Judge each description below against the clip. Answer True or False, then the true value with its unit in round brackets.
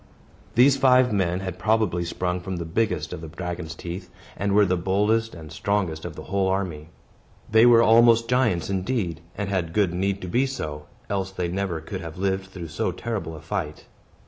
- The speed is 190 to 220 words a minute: True (195 wpm)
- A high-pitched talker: False (95 Hz)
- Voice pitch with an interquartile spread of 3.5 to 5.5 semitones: True (3.9 semitones)